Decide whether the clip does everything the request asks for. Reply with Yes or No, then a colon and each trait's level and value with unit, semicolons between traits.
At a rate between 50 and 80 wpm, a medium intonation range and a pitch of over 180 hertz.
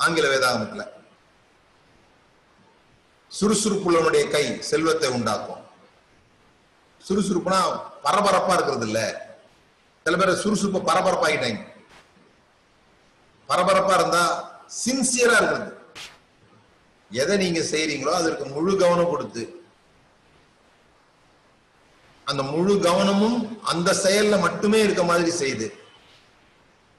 Yes: slow, 75 wpm; average, 3.3 semitones; high, 190 Hz